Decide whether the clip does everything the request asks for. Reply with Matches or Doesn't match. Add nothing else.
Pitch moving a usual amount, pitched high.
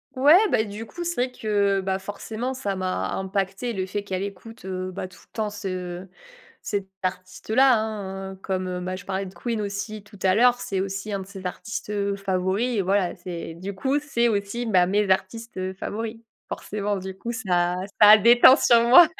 Matches